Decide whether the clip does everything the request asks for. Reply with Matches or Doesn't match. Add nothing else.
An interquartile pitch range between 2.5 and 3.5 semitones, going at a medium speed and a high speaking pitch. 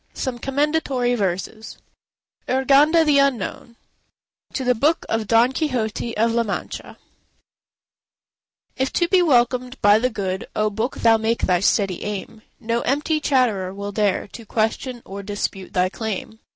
Doesn't match